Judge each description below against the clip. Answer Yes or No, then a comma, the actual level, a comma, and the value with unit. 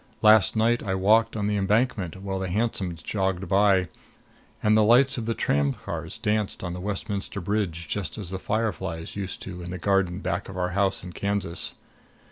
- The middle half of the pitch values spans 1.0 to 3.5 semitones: Yes, average, 2.8 semitones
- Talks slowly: No, average, 180 wpm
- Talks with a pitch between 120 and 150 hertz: No, very low, 95 Hz